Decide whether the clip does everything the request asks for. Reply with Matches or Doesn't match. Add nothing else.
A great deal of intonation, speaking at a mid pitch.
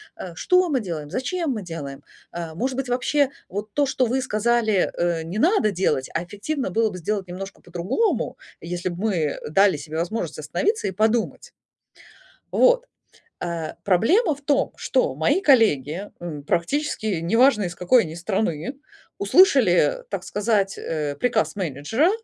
Doesn't match